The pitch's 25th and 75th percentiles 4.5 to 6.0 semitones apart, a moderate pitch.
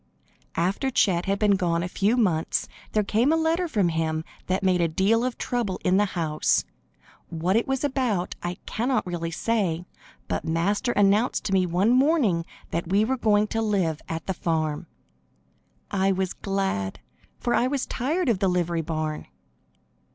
No: average, 5.1 semitones; high, 195 Hz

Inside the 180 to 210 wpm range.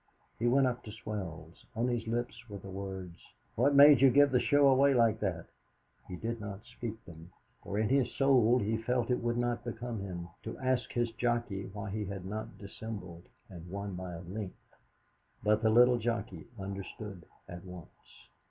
Yes: average, 185 wpm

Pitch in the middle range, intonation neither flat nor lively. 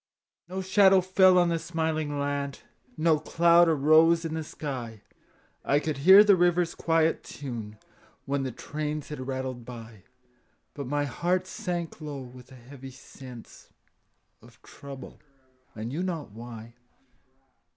Yes: medium, 150 Hz; average, 4.5 semitones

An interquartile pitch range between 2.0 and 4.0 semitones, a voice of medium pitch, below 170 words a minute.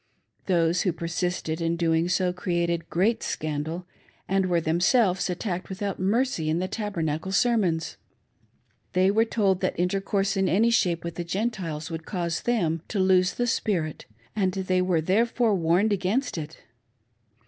Yes: average, 3.0 semitones; medium, 180 Hz; average, 150 wpm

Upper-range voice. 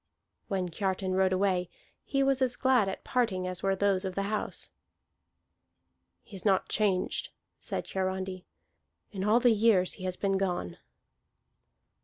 Yes: high, 195 Hz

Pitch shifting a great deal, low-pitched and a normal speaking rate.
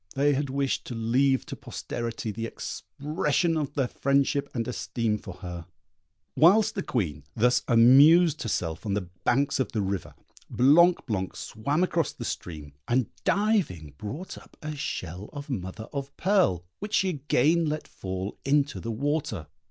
Yes: wide, 6.0 semitones; low, 130 Hz; average, 160 wpm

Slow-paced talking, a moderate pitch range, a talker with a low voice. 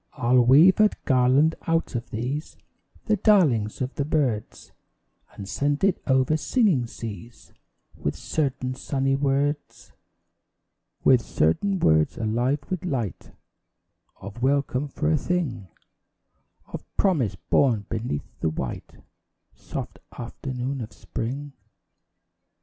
Yes: slow, 115 wpm; average, 4.2 semitones; low, 130 Hz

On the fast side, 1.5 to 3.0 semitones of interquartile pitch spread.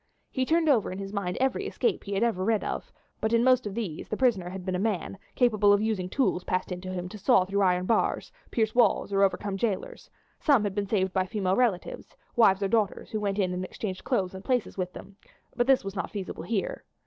No: fast, 240 wpm; average, 3.5 semitones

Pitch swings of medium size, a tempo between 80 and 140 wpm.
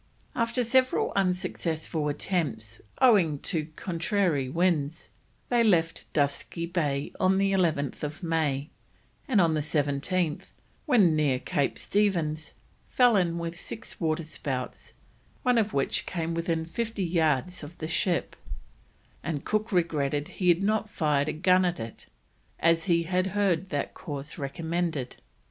Yes: average, 3.9 semitones; slow, 135 wpm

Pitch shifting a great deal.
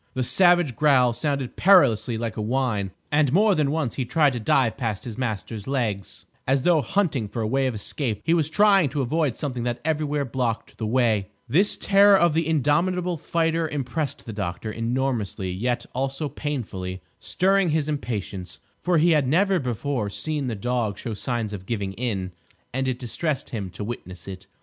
Yes: wide, 5.7 semitones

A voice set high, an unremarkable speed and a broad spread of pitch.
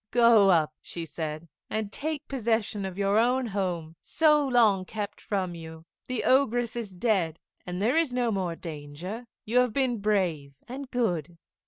Yes: high, 205 Hz; average, 165 wpm; wide, 5.9 semitones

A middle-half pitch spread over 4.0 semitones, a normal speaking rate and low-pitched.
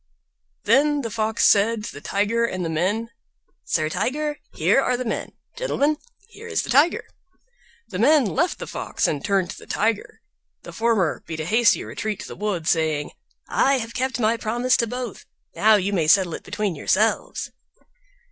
No: average, 4.9 semitones; average, 180 wpm; high, 220 Hz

